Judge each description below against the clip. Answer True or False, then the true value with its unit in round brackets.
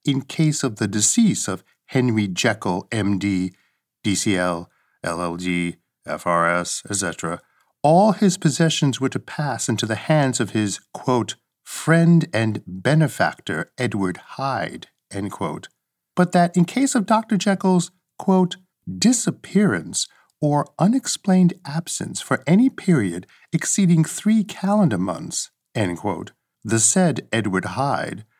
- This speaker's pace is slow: True (120 wpm)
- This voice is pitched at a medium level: True (145 Hz)